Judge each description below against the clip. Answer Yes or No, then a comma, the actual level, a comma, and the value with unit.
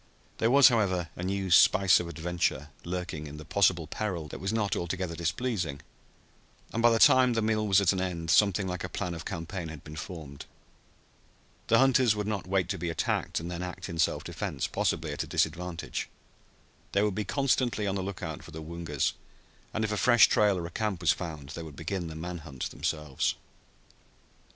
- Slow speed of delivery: No, average, 200 wpm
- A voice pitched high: No, very low, 90 Hz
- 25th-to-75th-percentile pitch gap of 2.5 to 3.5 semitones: No, average, 4.2 semitones